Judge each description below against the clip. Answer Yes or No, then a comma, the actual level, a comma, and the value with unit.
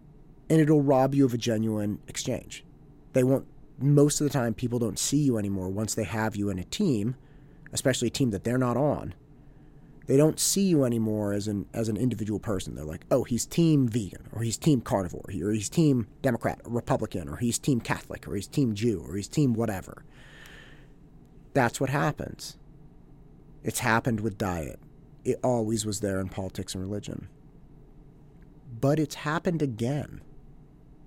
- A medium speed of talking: Yes, average, 175 wpm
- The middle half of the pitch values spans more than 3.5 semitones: Yes, average, 5.0 semitones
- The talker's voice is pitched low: Yes, low, 130 Hz